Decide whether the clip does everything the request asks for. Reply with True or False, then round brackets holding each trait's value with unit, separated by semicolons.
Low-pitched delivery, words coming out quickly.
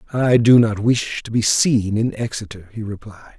False (110 Hz; 195 wpm)